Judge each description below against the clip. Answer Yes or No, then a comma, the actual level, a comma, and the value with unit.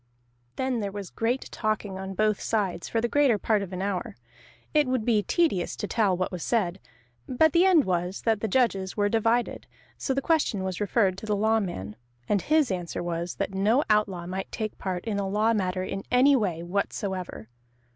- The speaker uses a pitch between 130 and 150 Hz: No, high, 205 Hz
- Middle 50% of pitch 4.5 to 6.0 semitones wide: No, average, 3.7 semitones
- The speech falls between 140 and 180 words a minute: No, average, 195 wpm